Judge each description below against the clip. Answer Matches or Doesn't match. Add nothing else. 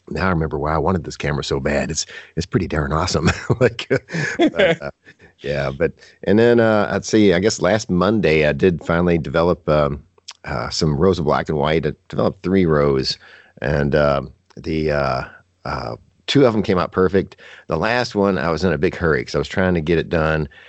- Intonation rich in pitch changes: Doesn't match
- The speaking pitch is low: Matches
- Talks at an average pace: Doesn't match